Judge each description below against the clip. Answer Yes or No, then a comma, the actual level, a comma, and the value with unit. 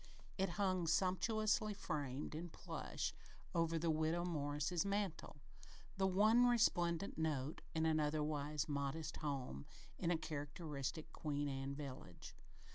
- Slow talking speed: Yes, slow, 120 wpm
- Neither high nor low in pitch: Yes, medium, 160 Hz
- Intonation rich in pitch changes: No, average, 3.7 semitones